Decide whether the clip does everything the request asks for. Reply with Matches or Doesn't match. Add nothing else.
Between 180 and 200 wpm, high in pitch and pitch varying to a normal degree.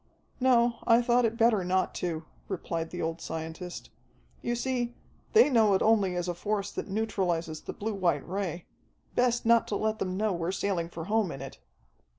Matches